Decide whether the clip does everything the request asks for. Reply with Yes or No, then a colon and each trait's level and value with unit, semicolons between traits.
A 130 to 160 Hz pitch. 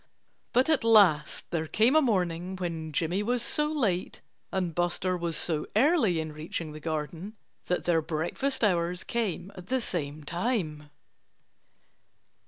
No: medium, 175 Hz